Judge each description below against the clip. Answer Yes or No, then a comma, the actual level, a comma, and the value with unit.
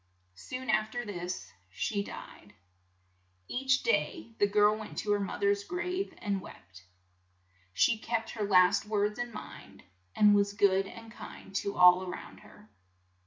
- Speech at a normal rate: Yes, average, 160 wpm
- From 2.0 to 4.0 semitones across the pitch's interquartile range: Yes, average, 2.8 semitones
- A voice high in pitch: Yes, high, 205 Hz